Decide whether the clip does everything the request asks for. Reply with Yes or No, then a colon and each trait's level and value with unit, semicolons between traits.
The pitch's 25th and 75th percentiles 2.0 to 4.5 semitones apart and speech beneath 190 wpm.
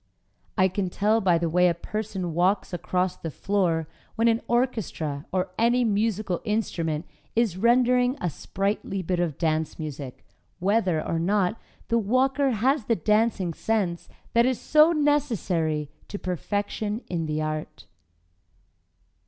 No: average, 5.1 semitones; average, 140 wpm